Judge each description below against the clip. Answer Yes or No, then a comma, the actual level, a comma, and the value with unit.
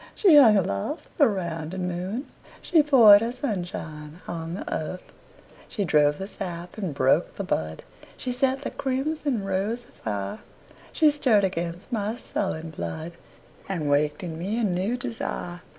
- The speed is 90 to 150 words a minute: Yes, slow, 135 wpm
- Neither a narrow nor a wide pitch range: No, wide, 6.5 semitones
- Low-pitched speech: No, high, 190 Hz